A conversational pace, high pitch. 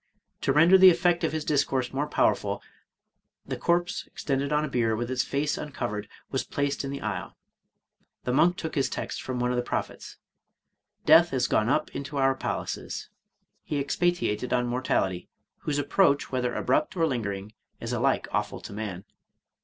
No: average, 180 wpm; low, 135 Hz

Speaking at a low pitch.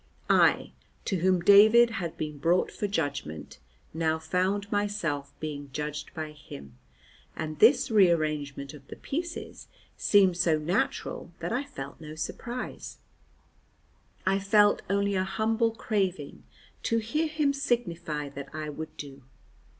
No: medium, 180 Hz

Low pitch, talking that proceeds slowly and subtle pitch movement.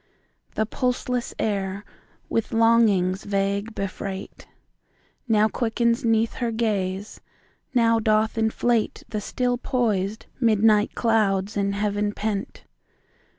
No: high, 215 Hz; slow, 95 wpm; narrow, 2.3 semitones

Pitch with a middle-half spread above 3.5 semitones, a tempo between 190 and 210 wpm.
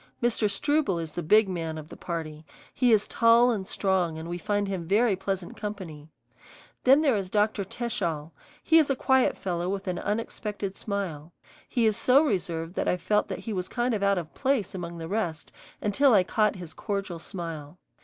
Yes: average, 4.4 semitones; average, 195 wpm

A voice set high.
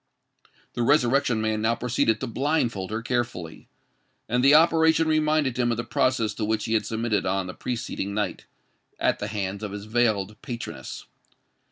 No: low, 115 Hz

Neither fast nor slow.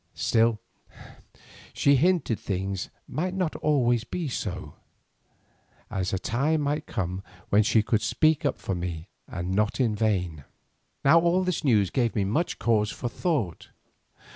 Yes: average, 145 wpm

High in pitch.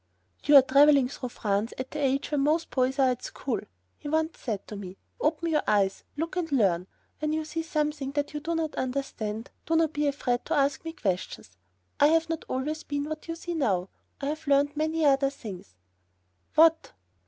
Yes: very high, 285 Hz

